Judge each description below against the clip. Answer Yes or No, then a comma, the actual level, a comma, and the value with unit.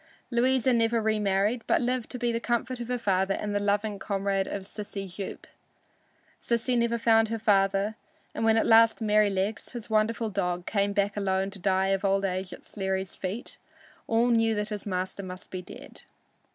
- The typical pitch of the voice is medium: No, high, 210 Hz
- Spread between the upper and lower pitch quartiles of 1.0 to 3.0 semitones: Yes, average, 2.7 semitones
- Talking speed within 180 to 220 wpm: Yes, average, 185 wpm